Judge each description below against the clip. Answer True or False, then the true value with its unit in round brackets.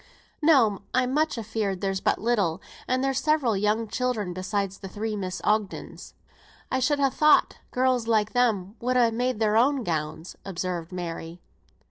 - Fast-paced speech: False (160 wpm)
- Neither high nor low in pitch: False (215 Hz)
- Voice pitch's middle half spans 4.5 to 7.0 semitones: True (4.9 semitones)